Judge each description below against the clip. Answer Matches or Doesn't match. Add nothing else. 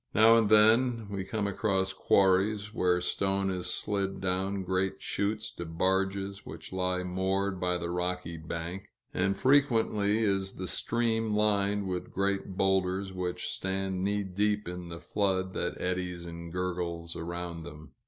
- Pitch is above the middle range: Doesn't match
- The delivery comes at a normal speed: Matches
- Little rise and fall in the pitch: Matches